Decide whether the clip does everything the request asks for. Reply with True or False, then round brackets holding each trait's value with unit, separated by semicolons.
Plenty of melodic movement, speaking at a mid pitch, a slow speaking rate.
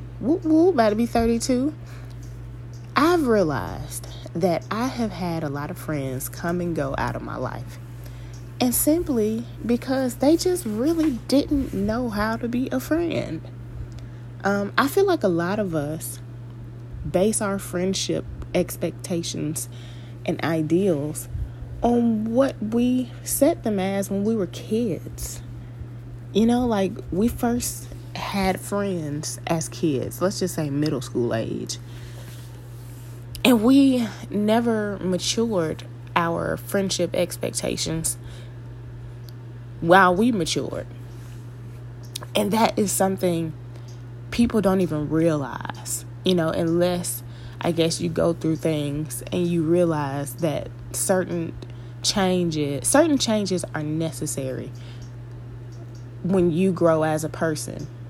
True (8.6 semitones; 155 Hz; 120 wpm)